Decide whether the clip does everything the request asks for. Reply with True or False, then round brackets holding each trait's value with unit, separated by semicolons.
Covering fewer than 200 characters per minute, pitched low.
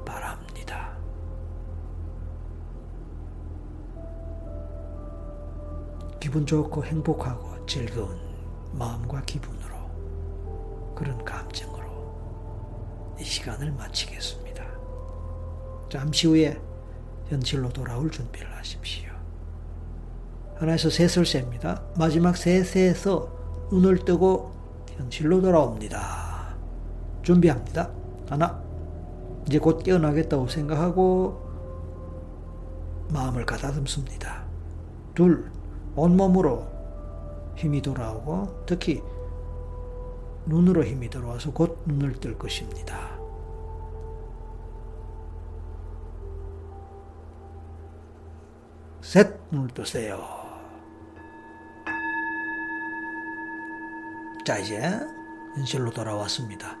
True (170 characters per minute; 90 Hz)